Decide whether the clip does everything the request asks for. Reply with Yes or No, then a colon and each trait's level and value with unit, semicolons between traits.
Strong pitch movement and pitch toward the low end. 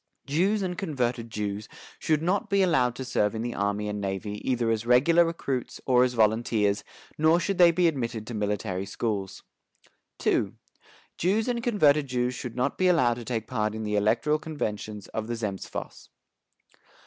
Yes: wide, 6.7 semitones; low, 120 Hz